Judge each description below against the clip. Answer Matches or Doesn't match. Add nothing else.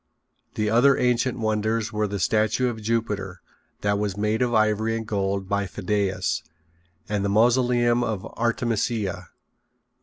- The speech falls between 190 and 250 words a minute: Doesn't match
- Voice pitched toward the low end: Matches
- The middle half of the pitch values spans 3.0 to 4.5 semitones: Doesn't match